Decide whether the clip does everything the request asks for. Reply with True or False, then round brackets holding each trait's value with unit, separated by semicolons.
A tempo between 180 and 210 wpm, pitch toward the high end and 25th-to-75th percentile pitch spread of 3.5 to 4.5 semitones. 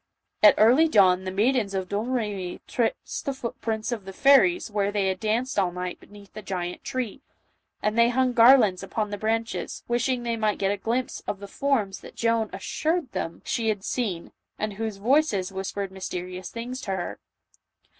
True (185 wpm; 215 Hz; 3.8 semitones)